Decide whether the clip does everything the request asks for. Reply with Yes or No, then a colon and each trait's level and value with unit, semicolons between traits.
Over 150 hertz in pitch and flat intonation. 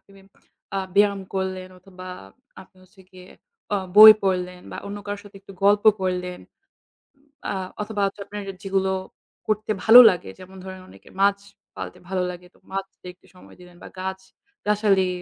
Yes: high, 190 Hz; narrow, 1.7 semitones